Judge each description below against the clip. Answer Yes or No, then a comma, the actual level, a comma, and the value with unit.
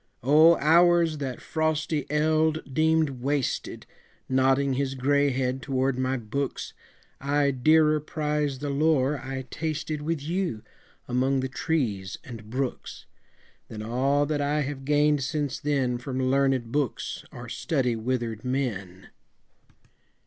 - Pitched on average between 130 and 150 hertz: Yes, medium, 140 Hz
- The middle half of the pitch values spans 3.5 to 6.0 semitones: No, average, 2.7 semitones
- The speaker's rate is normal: No, slow, 125 wpm